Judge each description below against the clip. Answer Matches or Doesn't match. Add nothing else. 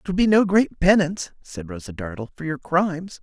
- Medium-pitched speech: Matches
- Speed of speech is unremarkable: Doesn't match